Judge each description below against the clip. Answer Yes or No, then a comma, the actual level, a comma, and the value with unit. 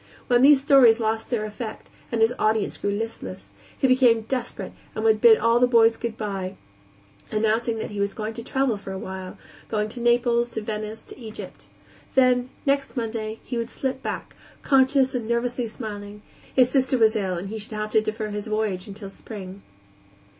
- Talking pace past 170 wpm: Yes, average, 190 wpm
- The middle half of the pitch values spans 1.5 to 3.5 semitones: Yes, narrow, 2.4 semitones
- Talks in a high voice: Yes, high, 225 Hz